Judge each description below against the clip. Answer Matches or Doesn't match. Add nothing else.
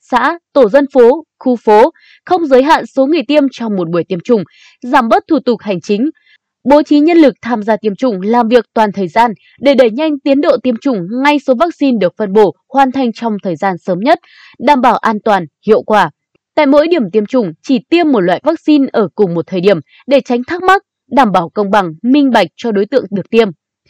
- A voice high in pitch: Matches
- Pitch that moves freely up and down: Matches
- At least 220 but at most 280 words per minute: Matches